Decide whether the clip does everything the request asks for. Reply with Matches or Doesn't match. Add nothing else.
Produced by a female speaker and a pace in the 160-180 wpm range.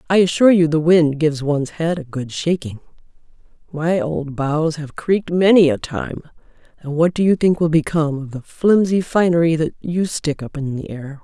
Doesn't match